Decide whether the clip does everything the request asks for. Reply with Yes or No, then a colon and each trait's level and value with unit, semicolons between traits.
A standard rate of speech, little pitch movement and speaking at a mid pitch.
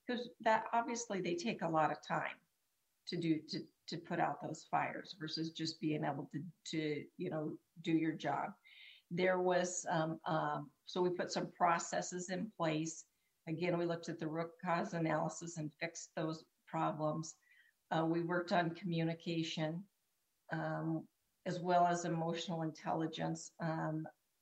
Yes: average, 155 wpm; narrow, 2.0 semitones; medium, 165 Hz